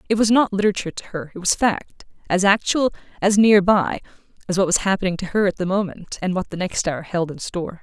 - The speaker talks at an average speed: No, fast, 240 wpm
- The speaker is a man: No, female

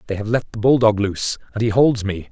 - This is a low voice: Yes, low, 110 Hz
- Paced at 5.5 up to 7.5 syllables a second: Yes, 6.0 syllables/s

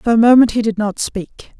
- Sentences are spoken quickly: Yes, fast, 265 wpm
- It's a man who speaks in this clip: No, female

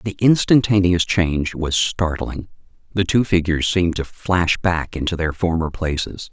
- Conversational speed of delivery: Yes, average, 150 wpm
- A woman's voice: No, male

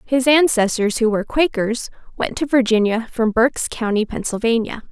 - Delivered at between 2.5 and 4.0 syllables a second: No, 4.9 syllables/s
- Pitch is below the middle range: No, high, 235 Hz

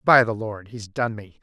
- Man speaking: Yes, male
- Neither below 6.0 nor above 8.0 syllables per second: No, 4.5 syllables/s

